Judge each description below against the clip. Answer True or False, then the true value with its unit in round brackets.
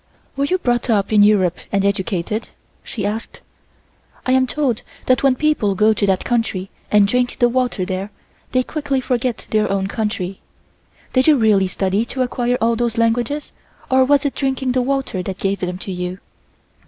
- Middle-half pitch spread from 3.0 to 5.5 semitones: True (4.6 semitones)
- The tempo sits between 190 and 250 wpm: False (180 wpm)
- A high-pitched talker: True (230 Hz)